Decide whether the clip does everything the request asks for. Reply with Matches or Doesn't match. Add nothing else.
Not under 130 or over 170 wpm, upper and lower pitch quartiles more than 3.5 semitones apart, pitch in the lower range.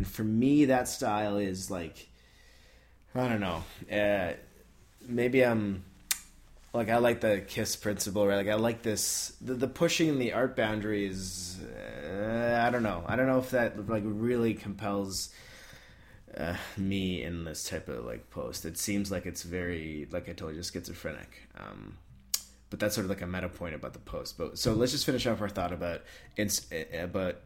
Doesn't match